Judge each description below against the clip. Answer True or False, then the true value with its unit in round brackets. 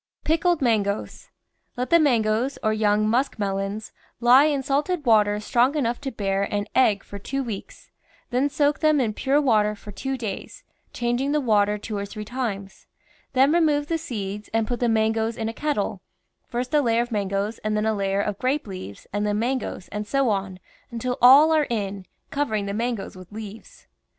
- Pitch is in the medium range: False (225 Hz)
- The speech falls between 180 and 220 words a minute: True (190 wpm)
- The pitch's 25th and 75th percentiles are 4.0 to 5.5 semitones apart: True (4.5 semitones)